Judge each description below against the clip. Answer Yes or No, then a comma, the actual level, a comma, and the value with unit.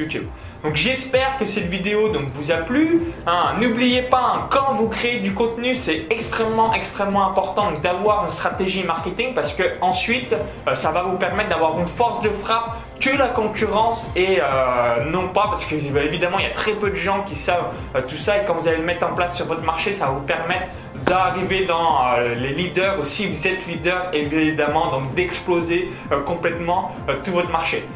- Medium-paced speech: Yes, average, 210 wpm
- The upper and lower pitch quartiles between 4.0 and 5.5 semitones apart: Yes, average, 4.6 semitones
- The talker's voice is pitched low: No, medium, 180 Hz